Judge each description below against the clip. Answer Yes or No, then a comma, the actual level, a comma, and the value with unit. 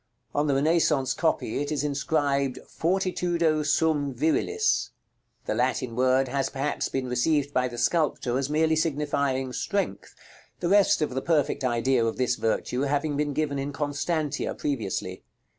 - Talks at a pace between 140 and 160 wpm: Yes, average, 150 wpm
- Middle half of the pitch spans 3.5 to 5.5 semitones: No, average, 3.0 semitones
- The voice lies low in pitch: No, medium, 145 Hz